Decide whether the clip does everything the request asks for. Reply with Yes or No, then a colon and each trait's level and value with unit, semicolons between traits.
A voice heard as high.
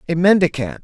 No: medium, 165 Hz